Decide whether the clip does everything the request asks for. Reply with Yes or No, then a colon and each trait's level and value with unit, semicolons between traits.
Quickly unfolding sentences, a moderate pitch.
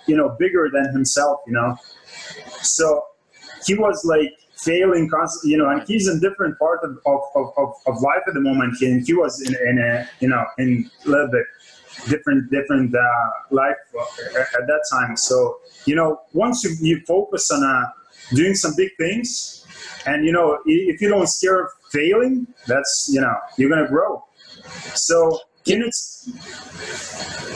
No: average, 170 wpm; medium, 160 Hz